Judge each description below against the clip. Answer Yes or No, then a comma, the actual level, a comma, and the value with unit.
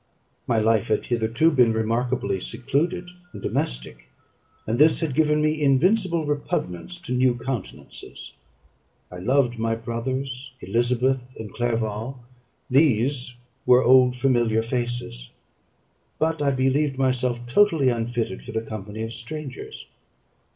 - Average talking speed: No, slow, 125 wpm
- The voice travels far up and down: No, average, 3.4 semitones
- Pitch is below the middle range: Yes, low, 125 Hz